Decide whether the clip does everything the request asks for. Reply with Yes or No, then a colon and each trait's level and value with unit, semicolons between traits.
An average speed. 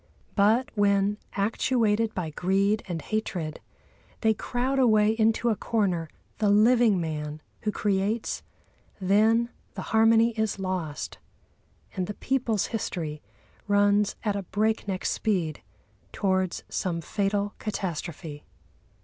No: slow, 115 wpm